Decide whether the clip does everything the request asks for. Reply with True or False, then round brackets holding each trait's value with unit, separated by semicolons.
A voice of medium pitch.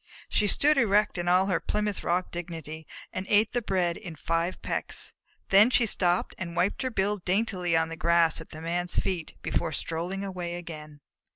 True (180 Hz)